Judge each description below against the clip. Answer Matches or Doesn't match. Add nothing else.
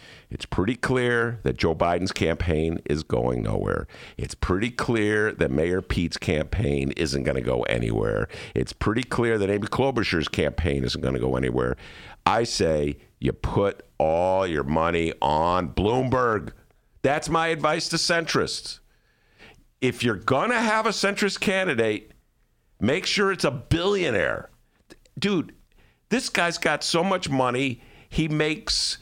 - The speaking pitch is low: Matches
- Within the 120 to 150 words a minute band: Matches